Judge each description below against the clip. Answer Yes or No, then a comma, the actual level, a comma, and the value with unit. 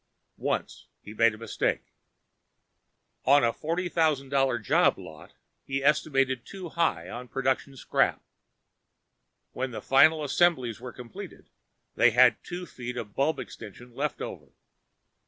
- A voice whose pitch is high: No, low, 130 Hz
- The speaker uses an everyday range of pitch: Yes, average, 4.0 semitones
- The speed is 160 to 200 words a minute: No, slow, 135 wpm